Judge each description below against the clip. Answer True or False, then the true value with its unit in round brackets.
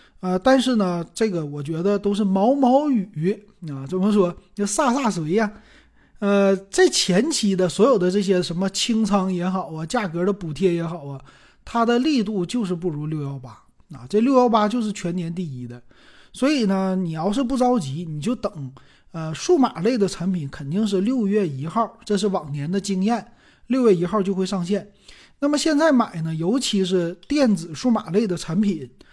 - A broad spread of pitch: False (4.5 semitones)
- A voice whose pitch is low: False (195 Hz)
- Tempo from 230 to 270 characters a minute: True (265 characters per minute)